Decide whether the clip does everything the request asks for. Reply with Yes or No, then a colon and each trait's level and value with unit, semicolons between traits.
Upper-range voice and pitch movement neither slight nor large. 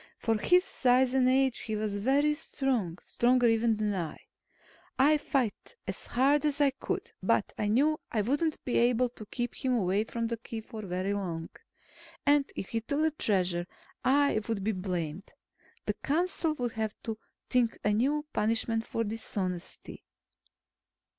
Yes: high, 230 Hz; average, 4.4 semitones